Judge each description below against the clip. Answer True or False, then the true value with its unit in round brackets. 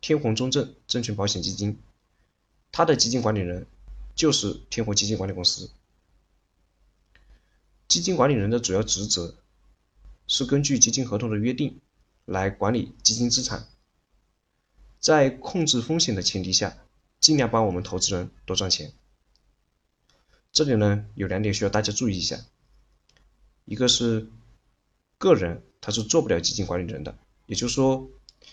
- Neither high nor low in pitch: False (105 Hz)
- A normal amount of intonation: True (5.0 semitones)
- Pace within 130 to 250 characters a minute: True (225 characters per minute)